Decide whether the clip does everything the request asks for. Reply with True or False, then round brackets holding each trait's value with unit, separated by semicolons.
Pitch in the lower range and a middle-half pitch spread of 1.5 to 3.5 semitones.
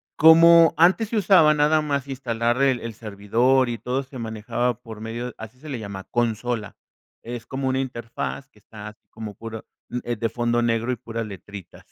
True (120 Hz; 3.2 semitones)